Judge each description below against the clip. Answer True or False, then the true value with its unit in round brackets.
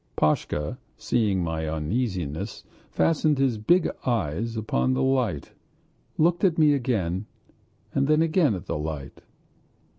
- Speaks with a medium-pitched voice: False (115 Hz)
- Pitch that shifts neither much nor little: False (8.8 semitones)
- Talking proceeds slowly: True (120 wpm)